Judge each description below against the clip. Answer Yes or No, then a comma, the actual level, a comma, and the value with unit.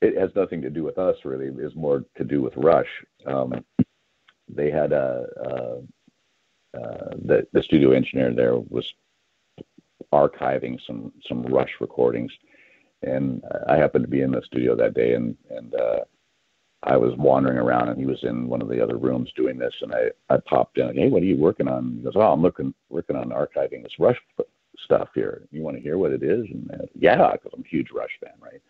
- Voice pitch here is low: Yes, very low, 65 Hz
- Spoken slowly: No, fast, 205 wpm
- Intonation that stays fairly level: Yes, narrow, 1.7 semitones